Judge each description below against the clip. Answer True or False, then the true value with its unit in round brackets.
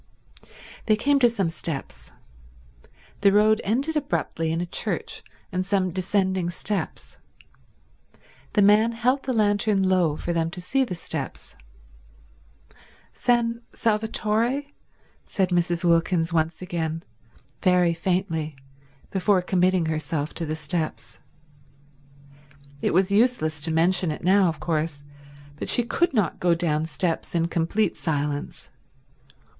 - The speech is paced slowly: True (125 wpm)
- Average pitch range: True (4.3 semitones)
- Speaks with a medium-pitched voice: True (180 Hz)